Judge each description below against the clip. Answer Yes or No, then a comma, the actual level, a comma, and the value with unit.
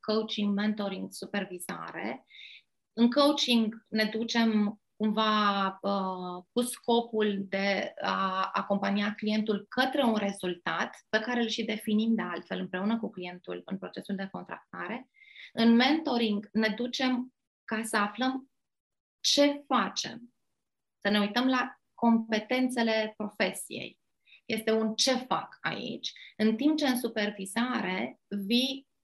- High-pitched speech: Yes, high, 220 Hz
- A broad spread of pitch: No, average, 3.3 semitones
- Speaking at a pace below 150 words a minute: Yes, average, 120 wpm